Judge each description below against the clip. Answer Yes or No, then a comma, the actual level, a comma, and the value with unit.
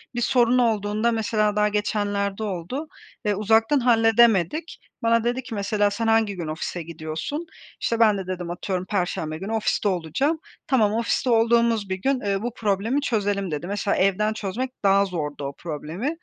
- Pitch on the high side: Yes, high, 210 Hz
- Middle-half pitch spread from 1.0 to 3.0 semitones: No, average, 3.5 semitones